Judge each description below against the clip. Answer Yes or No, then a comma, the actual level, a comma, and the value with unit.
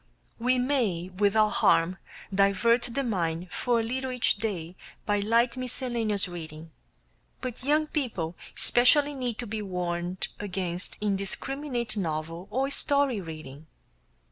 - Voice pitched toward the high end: Yes, high, 210 Hz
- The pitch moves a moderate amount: No, wide, 5.9 semitones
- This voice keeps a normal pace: No, slow, 125 wpm